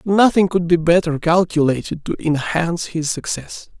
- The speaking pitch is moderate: Yes, medium, 170 Hz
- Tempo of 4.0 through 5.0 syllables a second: Yes, 4.7 syllables/s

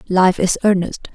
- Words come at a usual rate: Yes, average, 155 wpm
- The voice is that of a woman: Yes, female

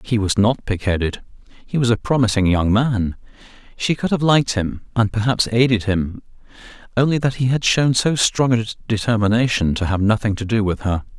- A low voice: Yes, low, 110 Hz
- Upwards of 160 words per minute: Yes, average, 180 wpm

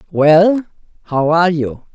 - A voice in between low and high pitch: Yes, medium, 165 Hz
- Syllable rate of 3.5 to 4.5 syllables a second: Yes, 3.9 syllables/s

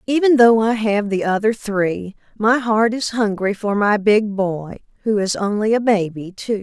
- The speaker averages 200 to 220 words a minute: No, average, 190 wpm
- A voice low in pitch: No, high, 210 Hz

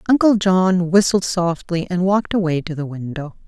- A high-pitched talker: No, medium, 180 Hz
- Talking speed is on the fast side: No, average, 175 wpm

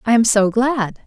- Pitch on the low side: No, high, 225 Hz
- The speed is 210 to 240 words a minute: Yes, fast, 225 wpm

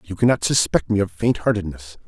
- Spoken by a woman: No, male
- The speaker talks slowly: No, fast, 205 wpm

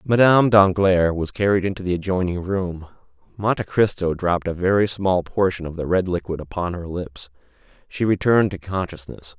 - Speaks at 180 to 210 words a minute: No, average, 165 wpm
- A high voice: No, very low, 90 Hz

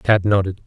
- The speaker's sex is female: No, male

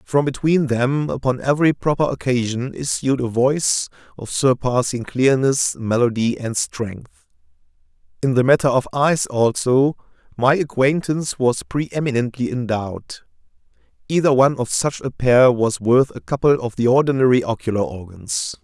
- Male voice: Yes, male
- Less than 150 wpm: Yes, average, 140 wpm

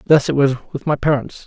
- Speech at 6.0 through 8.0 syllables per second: Yes, 6.2 syllables/s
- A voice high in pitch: No, medium, 140 Hz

